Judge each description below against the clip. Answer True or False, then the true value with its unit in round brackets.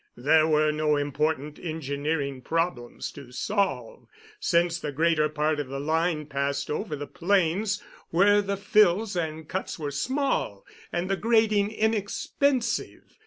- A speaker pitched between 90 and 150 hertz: False (160 Hz)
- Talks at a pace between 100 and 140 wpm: True (135 wpm)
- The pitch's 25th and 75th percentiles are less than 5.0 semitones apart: False (5.3 semitones)